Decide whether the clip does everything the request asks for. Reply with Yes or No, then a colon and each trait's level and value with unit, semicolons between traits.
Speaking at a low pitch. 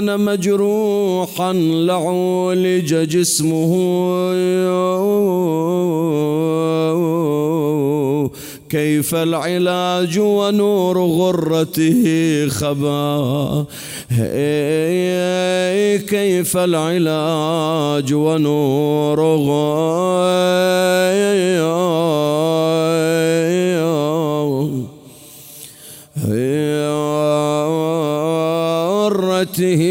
No: medium, 160 Hz